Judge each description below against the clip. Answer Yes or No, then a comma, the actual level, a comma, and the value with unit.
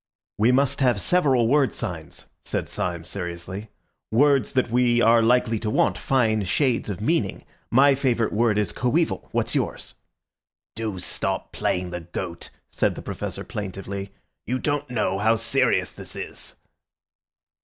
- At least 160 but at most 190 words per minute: No, average, 145 wpm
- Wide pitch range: No, average, 4.6 semitones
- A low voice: Yes, low, 115 Hz